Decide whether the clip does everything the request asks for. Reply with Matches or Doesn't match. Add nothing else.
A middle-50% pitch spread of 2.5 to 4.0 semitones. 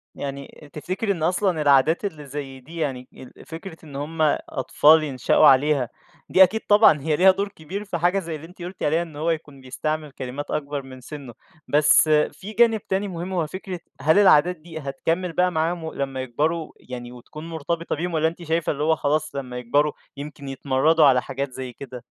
Matches